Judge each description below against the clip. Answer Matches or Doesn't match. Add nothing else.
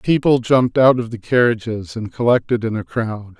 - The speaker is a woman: Doesn't match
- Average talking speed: Matches